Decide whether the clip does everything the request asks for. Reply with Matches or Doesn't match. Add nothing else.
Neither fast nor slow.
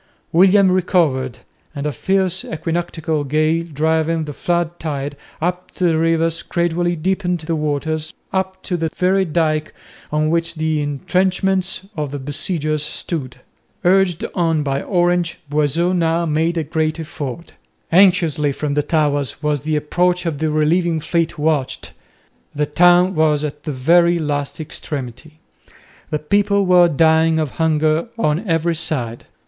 Matches